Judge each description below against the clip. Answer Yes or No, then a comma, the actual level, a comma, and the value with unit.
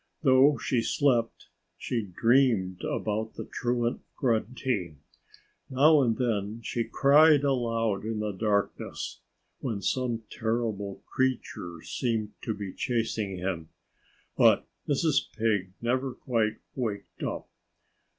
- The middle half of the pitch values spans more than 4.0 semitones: No, average, 3.7 semitones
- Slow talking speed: Yes, slow, 110 wpm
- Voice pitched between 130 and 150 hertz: No, low, 115 Hz